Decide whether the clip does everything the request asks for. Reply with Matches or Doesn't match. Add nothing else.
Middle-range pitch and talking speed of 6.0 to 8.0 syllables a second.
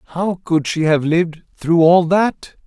Doesn't match